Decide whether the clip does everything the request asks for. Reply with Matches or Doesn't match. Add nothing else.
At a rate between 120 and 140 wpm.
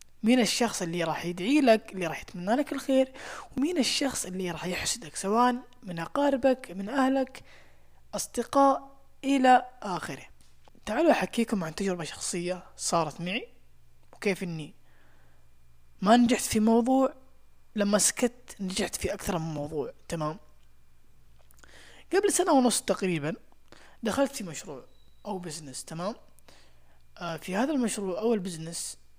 Matches